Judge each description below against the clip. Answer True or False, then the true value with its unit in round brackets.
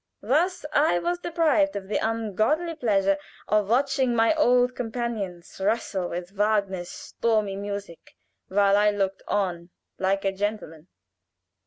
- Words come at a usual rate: False (130 wpm)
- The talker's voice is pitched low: False (210 Hz)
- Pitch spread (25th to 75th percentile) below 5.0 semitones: True (4.2 semitones)